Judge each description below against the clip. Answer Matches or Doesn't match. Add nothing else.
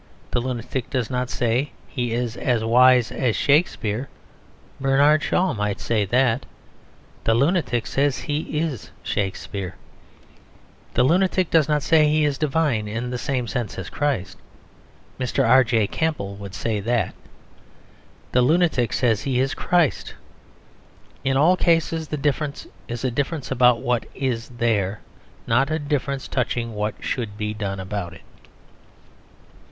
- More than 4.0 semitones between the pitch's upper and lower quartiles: Matches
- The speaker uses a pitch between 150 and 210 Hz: Doesn't match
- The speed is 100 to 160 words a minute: Matches